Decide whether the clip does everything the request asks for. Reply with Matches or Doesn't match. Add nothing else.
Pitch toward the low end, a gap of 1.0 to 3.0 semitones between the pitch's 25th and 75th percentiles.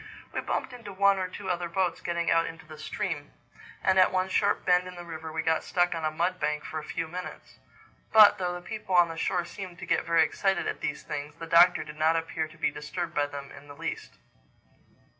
Doesn't match